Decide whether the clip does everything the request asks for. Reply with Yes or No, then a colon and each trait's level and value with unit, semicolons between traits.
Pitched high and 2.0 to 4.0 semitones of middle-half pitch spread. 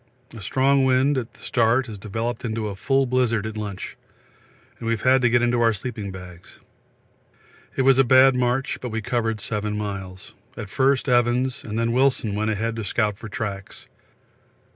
No: low, 115 Hz; average, 3.4 semitones